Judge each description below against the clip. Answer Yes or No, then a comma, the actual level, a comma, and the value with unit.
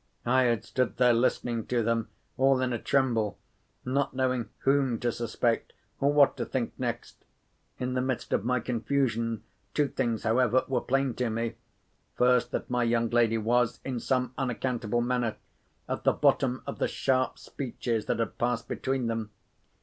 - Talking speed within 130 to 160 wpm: No, average, 170 wpm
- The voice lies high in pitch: No, low, 125 Hz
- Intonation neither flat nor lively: No, narrow, 1.9 semitones